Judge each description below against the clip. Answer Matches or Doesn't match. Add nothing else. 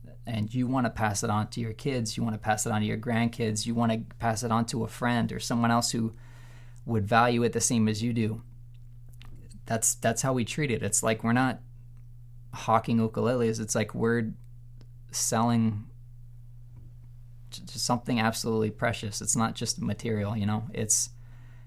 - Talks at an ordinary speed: Matches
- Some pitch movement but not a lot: Doesn't match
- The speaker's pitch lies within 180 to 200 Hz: Doesn't match